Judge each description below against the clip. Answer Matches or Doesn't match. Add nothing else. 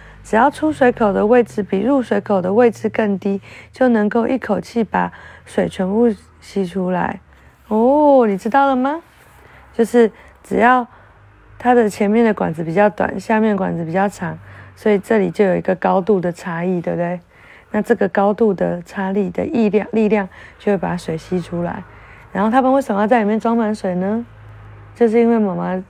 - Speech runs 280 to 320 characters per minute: Doesn't match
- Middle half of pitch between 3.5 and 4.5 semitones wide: Matches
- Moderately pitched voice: Doesn't match